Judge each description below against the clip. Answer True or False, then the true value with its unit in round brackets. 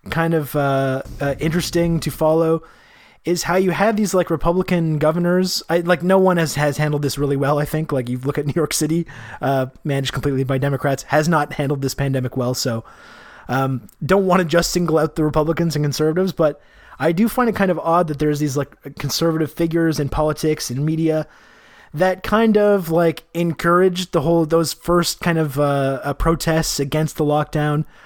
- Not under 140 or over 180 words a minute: False (195 wpm)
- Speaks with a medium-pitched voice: True (155 Hz)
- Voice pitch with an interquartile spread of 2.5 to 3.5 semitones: True (2.9 semitones)